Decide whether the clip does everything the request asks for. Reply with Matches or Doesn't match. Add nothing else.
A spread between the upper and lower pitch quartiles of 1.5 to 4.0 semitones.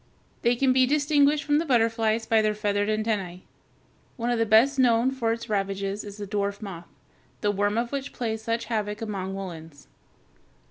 Matches